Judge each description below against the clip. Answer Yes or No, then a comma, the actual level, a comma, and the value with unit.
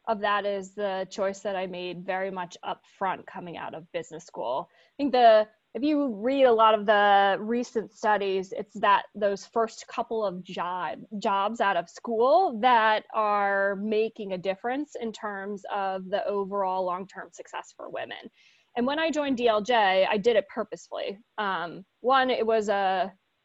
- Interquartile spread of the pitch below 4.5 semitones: Yes, average, 3.3 semitones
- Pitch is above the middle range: Yes, high, 210 Hz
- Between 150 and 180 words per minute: Yes, average, 175 wpm